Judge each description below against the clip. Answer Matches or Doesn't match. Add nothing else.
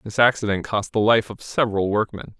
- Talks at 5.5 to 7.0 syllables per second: Matches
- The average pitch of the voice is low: Matches